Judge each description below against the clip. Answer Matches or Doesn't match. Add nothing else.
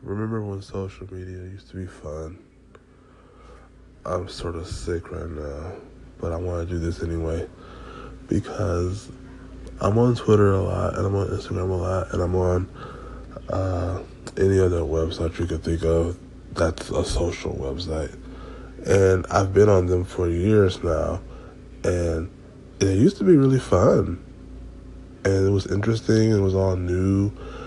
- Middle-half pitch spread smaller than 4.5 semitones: Matches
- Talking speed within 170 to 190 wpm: Doesn't match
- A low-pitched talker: Matches